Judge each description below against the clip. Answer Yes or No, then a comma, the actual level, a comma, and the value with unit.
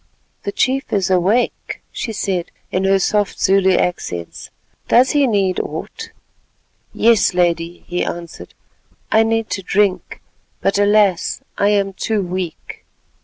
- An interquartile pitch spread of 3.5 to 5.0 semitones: No, average, 3.0 semitones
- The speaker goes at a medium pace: No, slow, 130 wpm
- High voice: Yes, high, 195 Hz